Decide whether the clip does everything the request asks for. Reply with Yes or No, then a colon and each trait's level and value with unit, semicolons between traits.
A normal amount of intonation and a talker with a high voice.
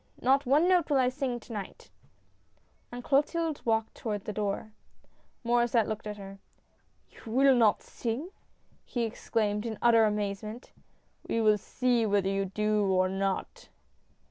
Yes: average, 3.3 semitones; high, 225 Hz